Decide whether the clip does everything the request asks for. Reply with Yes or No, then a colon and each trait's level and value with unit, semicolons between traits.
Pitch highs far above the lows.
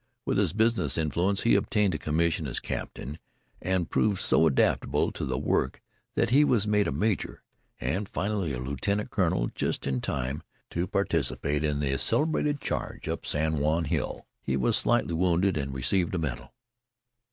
Yes: wide, 5.9 semitones